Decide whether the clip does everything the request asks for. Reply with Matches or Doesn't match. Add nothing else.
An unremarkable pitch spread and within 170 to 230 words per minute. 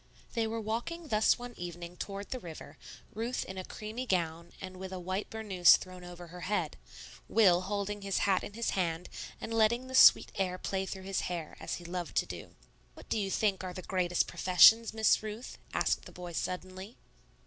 Matches